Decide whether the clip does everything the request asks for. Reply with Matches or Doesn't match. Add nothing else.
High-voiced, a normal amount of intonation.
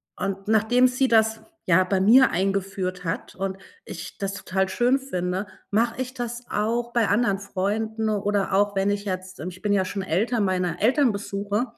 Matches